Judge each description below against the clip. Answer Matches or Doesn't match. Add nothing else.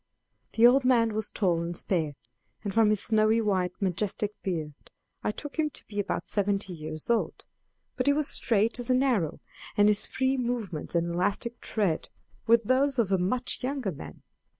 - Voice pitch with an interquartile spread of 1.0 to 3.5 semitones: Doesn't match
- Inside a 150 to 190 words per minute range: Matches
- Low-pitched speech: Doesn't match